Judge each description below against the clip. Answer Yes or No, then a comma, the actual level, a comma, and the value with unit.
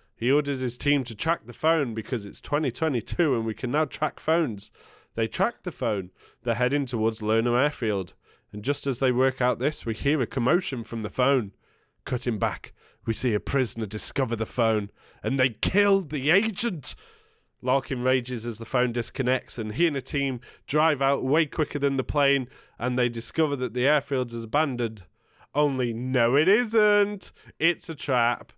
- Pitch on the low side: Yes, low, 130 Hz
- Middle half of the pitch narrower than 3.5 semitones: No, average, 3.8 semitones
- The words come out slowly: No, average, 185 wpm